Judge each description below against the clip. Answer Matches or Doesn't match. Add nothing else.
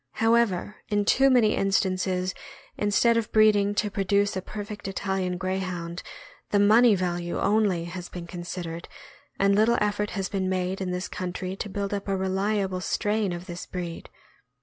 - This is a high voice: Matches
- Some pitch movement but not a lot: Doesn't match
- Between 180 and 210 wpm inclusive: Doesn't match